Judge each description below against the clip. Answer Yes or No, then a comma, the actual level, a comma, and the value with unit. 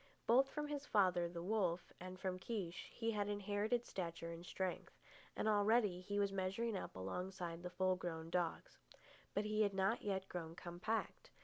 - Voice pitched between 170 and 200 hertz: Yes, high, 190 Hz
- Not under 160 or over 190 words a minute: Yes, average, 175 wpm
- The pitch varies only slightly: No, average, 3.1 semitones